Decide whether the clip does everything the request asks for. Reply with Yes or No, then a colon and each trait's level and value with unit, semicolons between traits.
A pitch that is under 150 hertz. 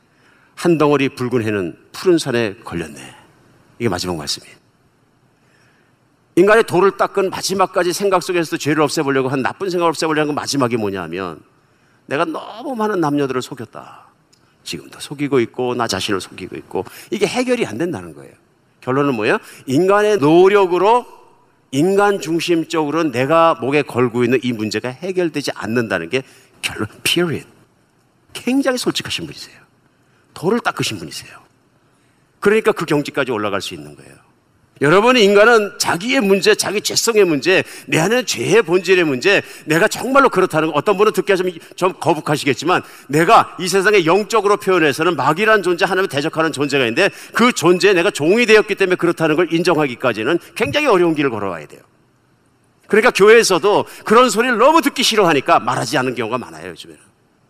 No: medium, 170 Hz